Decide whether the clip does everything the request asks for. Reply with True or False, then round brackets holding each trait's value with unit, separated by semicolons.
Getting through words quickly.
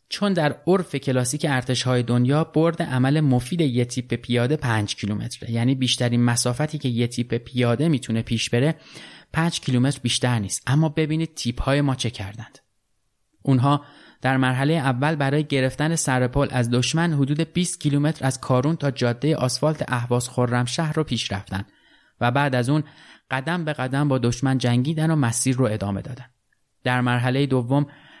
True (165 wpm)